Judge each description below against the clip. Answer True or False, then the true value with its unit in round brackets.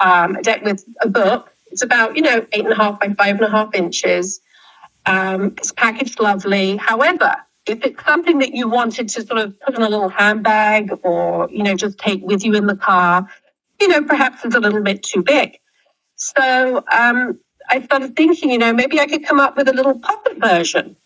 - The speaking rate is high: True (210 wpm)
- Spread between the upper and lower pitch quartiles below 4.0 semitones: False (5.1 semitones)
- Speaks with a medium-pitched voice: False (225 Hz)